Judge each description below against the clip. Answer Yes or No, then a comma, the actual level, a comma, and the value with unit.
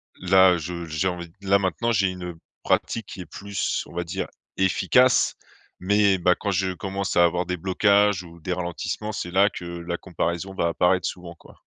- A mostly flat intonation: Yes, narrow, 2.1 semitones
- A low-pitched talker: Yes, very low, 90 Hz